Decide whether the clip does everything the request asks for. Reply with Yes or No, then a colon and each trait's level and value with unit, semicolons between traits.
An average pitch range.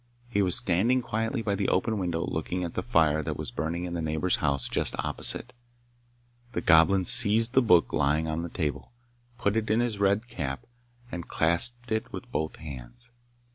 No: wide, 5.7 semitones